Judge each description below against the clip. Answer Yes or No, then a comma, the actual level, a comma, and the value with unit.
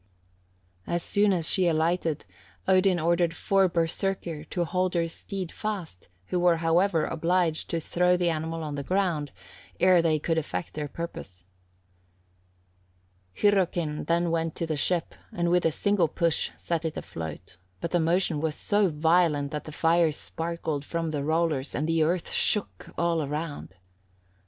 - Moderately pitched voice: Yes, medium, 165 Hz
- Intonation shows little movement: Yes, narrow, 2.2 semitones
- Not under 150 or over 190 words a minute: Yes, average, 155 wpm